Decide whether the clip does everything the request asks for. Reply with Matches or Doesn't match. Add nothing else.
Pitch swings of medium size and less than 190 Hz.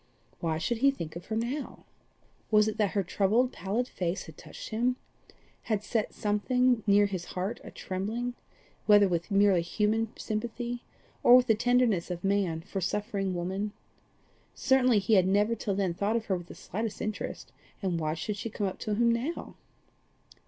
Doesn't match